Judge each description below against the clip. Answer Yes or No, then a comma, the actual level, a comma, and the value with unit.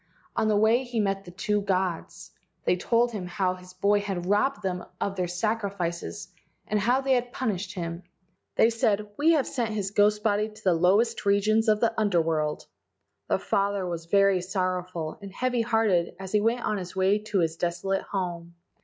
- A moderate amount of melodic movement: Yes, average, 3.1 semitones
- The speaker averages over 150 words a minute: Yes, average, 190 wpm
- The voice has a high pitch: Yes, high, 200 Hz